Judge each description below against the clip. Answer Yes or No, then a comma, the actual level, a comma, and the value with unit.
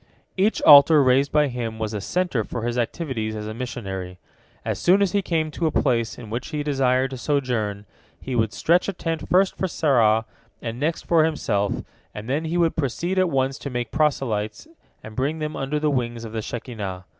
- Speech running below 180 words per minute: No, fast, 205 wpm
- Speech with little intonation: No, wide, 5.6 semitones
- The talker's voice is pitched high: No, low, 130 Hz